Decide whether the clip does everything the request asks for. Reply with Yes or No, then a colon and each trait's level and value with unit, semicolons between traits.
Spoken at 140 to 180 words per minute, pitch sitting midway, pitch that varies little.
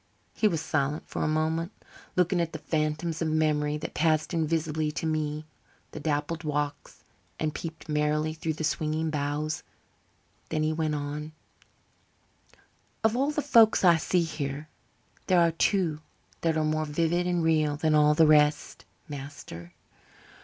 Yes: average, 150 wpm; medium, 155 Hz; narrow, 1.5 semitones